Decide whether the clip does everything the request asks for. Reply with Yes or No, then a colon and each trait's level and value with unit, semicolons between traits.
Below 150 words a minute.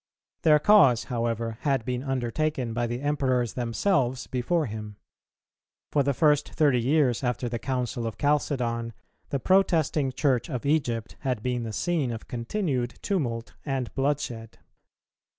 Yes: average, 140 wpm